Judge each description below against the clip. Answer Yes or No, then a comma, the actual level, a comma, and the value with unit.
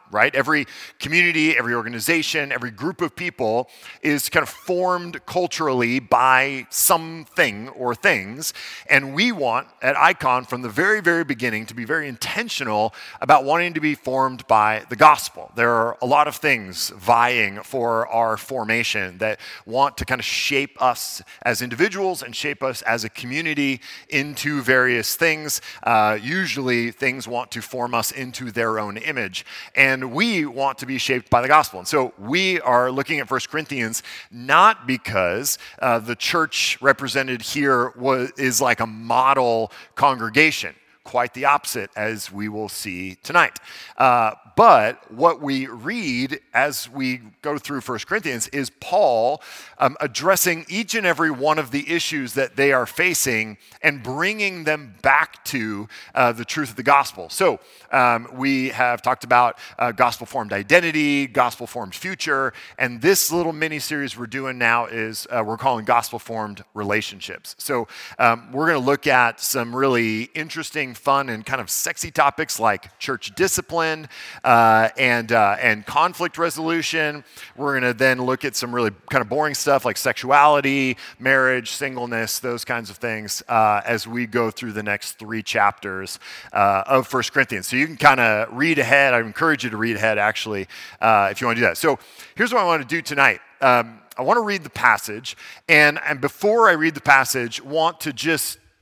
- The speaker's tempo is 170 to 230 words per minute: Yes, average, 175 wpm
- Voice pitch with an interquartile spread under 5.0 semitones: Yes, average, 4.4 semitones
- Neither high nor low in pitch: No, low, 130 Hz